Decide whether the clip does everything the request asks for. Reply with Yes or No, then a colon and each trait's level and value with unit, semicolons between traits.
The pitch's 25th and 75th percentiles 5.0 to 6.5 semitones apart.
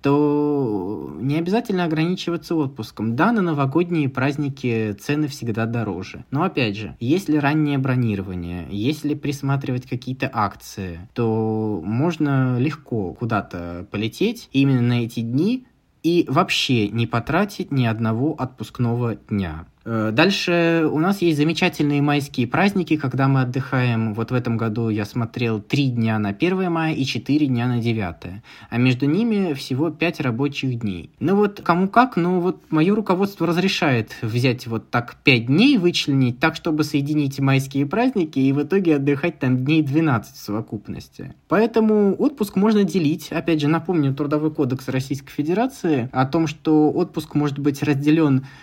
Yes: wide, 5.6 semitones